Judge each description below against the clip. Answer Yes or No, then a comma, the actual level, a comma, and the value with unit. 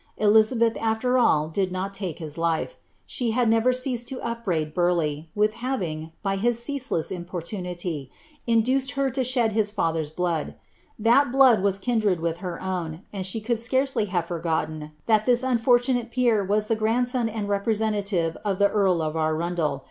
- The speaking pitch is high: Yes, high, 205 Hz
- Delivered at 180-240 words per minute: No, average, 170 wpm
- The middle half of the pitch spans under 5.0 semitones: No, wide, 5.5 semitones